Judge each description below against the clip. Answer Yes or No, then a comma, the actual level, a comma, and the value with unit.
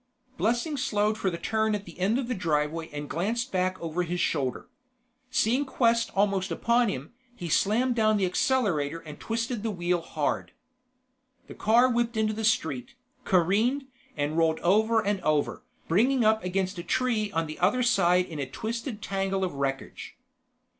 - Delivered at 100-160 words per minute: No, average, 170 wpm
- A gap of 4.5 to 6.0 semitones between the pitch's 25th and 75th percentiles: Yes, wide, 5.5 semitones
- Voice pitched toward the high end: Yes, high, 200 Hz